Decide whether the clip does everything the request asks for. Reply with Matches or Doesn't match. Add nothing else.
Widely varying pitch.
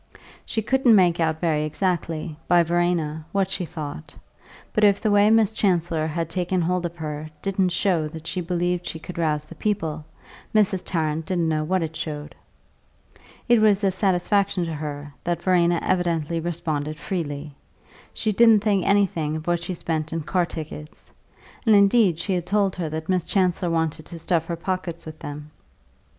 Doesn't match